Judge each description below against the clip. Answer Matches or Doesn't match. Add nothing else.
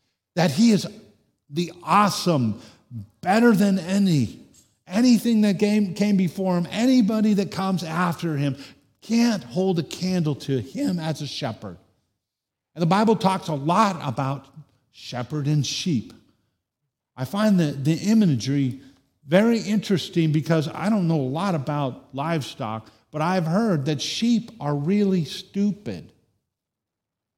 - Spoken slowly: Matches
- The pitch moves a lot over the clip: Matches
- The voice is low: Doesn't match